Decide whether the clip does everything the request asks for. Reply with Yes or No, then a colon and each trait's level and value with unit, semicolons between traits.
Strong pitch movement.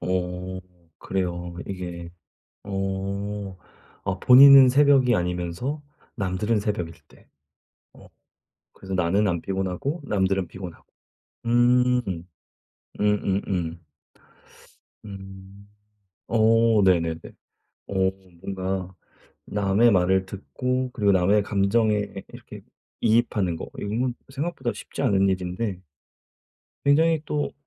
No: average, 4.0 semitones